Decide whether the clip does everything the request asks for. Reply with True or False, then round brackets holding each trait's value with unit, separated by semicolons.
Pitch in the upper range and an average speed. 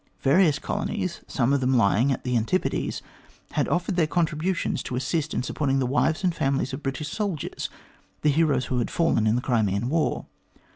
False (140 Hz; 185 wpm)